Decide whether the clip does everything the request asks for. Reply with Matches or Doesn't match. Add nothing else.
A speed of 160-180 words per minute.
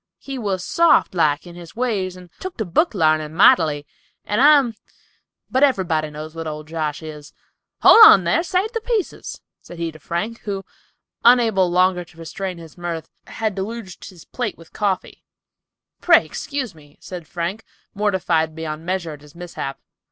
Matches